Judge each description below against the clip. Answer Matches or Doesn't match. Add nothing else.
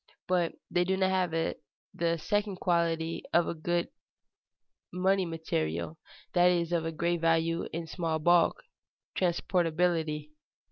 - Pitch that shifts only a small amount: Matches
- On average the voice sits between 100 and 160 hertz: Doesn't match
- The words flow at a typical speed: Doesn't match